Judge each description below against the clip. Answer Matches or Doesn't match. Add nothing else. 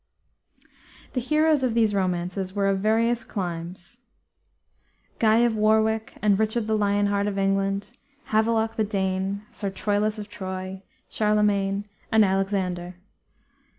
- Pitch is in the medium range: Doesn't match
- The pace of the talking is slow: Matches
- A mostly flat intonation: Matches